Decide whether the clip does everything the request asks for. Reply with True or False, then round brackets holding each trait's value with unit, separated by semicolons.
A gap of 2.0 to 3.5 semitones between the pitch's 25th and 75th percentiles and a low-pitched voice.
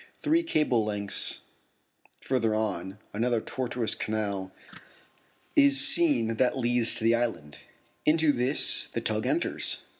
False (4.0 semitones; 120 Hz)